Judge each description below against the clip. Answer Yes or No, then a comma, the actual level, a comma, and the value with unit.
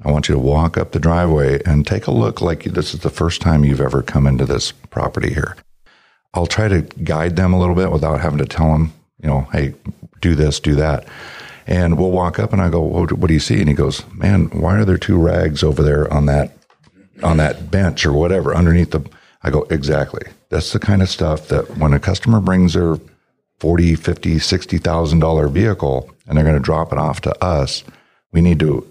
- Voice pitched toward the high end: No, very low, 80 Hz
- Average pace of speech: No, fast, 225 wpm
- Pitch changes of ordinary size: Yes, average, 3.1 semitones